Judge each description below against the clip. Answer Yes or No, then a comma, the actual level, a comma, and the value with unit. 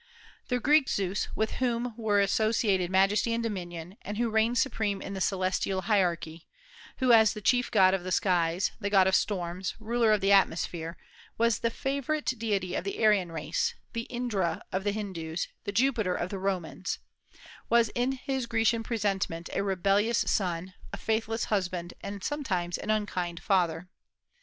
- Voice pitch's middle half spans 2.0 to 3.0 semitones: No, average, 3.8 semitones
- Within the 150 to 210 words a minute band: Yes, average, 165 wpm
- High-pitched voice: Yes, high, 200 Hz